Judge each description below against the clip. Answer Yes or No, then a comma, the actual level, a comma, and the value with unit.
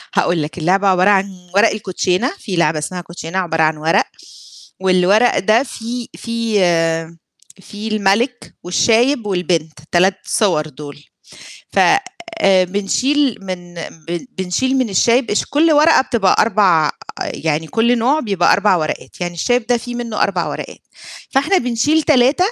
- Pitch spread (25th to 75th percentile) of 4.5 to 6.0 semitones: Yes, wide, 5.4 semitones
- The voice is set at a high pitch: Yes, high, 195 Hz